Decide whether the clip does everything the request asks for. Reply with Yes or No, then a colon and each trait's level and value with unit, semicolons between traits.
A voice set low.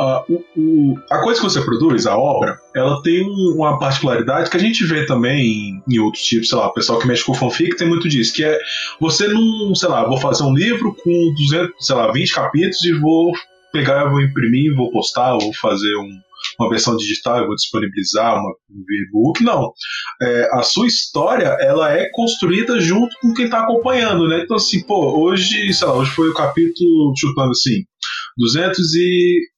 No: medium, 165 Hz